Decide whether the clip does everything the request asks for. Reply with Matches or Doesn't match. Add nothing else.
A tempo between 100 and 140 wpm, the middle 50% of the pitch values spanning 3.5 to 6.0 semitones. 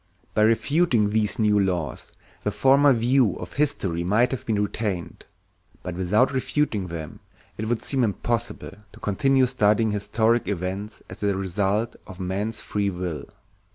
Doesn't match